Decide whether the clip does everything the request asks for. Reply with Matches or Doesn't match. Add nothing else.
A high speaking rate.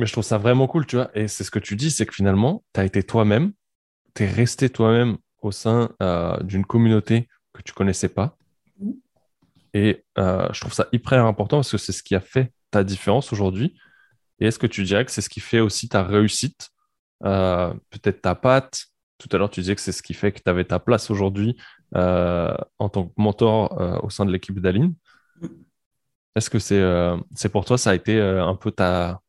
Matches